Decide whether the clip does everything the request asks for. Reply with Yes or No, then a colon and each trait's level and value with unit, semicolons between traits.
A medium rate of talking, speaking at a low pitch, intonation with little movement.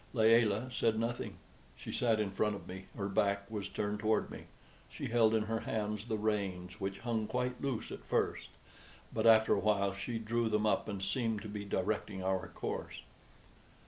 Yes: average, 185 wpm; low, 105 Hz; narrow, 2.2 semitones